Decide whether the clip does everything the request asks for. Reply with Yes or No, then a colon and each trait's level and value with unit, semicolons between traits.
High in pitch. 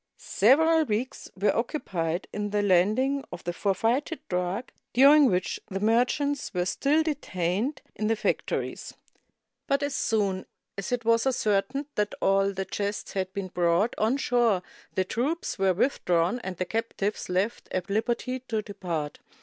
Yes: high, 210 Hz